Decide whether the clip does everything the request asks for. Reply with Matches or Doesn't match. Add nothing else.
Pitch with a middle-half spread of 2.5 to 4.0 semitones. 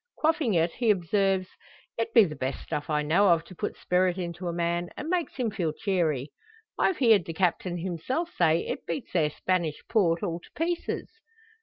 Doesn't match